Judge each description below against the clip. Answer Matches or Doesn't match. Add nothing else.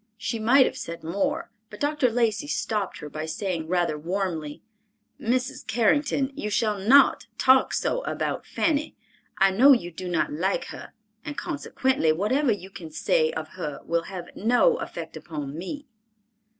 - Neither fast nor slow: Matches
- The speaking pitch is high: Matches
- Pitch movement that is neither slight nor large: Doesn't match